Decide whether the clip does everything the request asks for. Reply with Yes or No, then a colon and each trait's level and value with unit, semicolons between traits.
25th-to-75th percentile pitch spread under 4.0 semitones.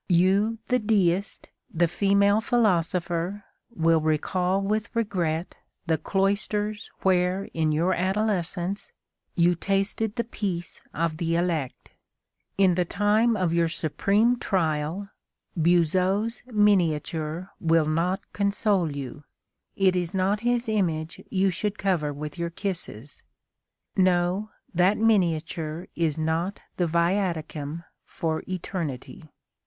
Yes: average, 3.5 semitones